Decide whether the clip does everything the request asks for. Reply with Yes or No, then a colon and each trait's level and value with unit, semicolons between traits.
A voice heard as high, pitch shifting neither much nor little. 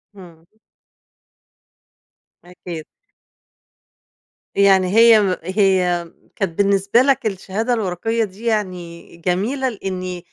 Yes: high, 195 Hz; average, 3.4 semitones